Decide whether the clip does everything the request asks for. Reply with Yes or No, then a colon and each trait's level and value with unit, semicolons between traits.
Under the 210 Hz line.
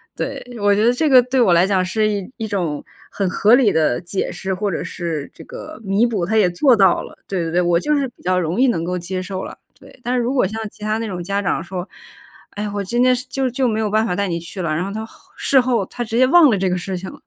Yes: high, 200 Hz